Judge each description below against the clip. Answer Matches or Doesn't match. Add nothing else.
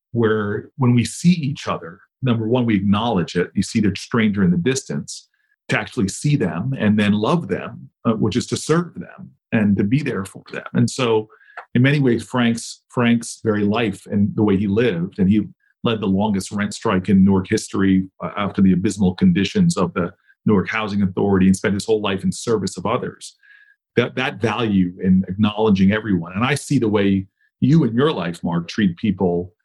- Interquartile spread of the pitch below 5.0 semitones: Doesn't match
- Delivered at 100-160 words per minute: Doesn't match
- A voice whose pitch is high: Doesn't match